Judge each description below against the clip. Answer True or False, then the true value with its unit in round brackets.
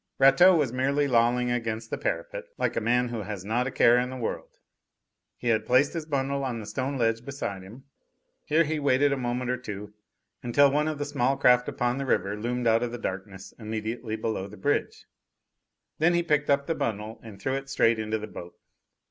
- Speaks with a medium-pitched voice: False (125 Hz)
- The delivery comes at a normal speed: False (210 wpm)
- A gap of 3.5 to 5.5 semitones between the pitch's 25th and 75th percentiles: True (3.8 semitones)